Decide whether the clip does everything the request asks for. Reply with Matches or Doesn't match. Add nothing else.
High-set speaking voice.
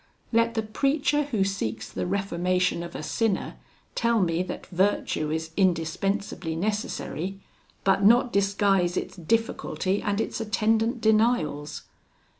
Matches